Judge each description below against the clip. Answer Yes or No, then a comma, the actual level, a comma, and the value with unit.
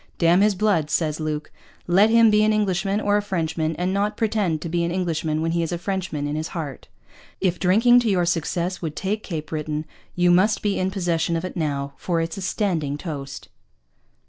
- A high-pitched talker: No, medium, 175 Hz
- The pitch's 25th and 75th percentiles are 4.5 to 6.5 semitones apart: No, average, 3.8 semitones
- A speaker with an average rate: No, fast, 210 wpm